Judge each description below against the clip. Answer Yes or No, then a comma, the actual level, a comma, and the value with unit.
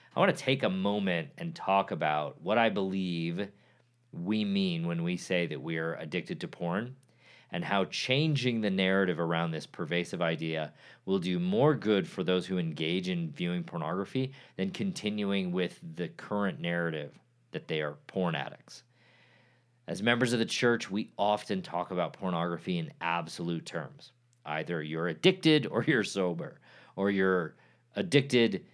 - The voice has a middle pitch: No, low, 105 Hz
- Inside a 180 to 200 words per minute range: No, average, 160 wpm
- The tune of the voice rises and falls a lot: Yes, wide, 7.2 semitones